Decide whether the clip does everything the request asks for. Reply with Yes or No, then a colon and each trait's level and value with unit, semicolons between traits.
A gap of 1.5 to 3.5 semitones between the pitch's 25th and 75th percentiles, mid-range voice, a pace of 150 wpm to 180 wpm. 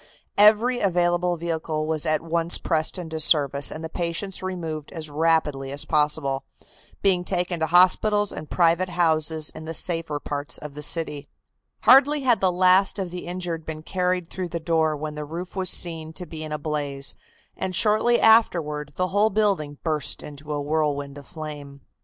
Yes: average, 3.2 semitones; medium, 165 Hz; average, 175 wpm